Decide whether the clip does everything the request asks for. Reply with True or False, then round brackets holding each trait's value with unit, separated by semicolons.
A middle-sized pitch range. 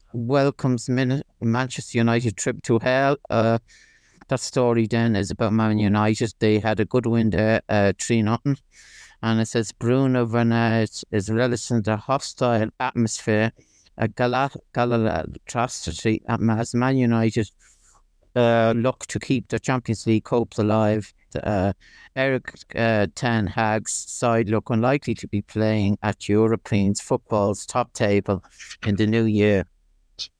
False (2.2 semitones)